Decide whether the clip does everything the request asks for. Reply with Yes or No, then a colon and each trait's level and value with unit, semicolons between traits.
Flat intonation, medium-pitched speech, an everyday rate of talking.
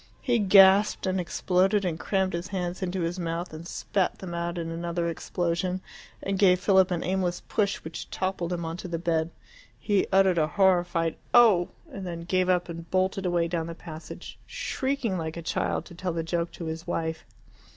Yes: narrow, 2.1 semitones; medium, 175 Hz; average, 195 wpm